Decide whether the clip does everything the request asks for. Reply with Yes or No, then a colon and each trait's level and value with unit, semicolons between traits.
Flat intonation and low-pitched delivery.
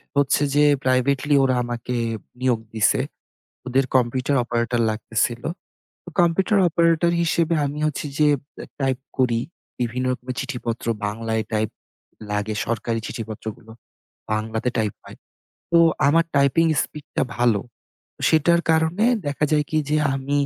No: average, 4.6 semitones; low, 130 Hz